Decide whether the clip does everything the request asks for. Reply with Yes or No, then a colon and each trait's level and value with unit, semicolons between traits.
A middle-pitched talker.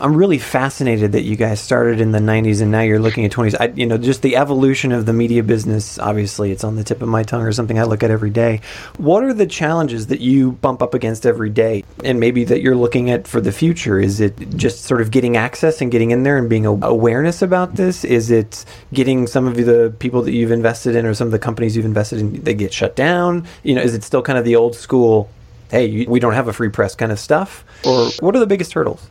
No: low, 115 Hz